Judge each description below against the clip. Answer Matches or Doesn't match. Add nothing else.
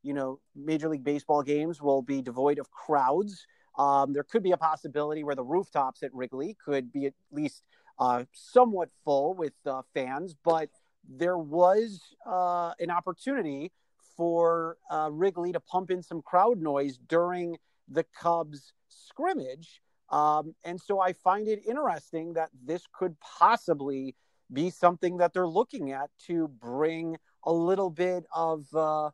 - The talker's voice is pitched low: Doesn't match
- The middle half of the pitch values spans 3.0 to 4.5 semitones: Matches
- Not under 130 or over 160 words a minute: Matches